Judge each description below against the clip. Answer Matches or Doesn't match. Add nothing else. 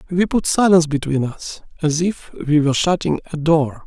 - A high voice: Doesn't match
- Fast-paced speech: Doesn't match